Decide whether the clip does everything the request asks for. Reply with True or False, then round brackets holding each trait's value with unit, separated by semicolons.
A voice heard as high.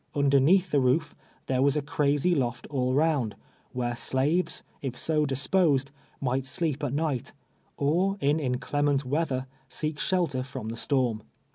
False (140 Hz)